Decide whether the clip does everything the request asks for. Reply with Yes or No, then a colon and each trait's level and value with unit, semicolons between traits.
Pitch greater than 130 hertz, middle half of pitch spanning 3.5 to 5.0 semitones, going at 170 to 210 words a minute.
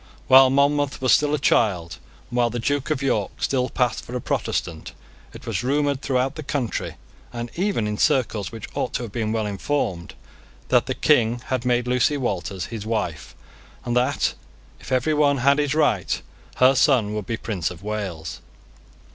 No: low, 125 Hz; average, 4.4 semitones; average, 180 wpm